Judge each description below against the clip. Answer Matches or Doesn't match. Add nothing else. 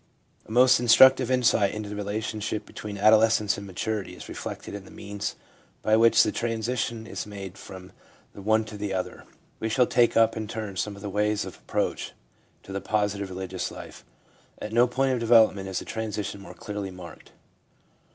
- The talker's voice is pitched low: Matches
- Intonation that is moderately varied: Doesn't match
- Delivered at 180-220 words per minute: Matches